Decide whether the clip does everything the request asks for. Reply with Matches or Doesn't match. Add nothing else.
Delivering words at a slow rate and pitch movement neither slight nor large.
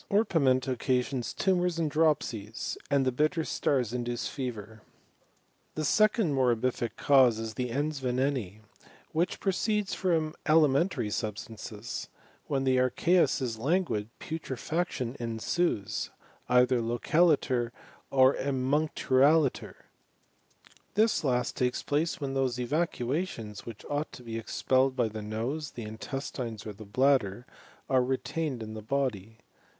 Matches